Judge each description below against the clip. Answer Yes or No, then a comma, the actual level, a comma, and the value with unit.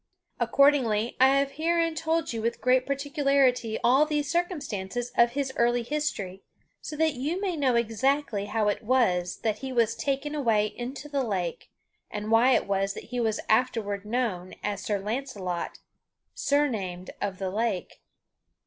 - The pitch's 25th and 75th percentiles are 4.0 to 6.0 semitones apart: Yes, average, 5.1 semitones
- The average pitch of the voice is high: Yes, high, 240 Hz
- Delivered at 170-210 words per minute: No, average, 155 wpm